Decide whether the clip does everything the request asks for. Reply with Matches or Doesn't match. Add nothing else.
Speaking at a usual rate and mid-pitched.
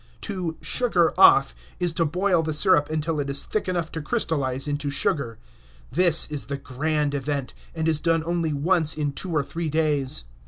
Matches